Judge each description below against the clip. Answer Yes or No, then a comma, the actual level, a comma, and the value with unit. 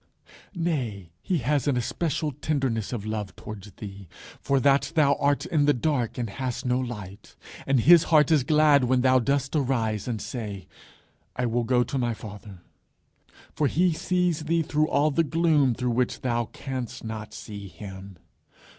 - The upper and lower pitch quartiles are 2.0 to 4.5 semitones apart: No, average, 5.0 semitones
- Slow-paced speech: No, average, 170 wpm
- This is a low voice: Yes, low, 130 Hz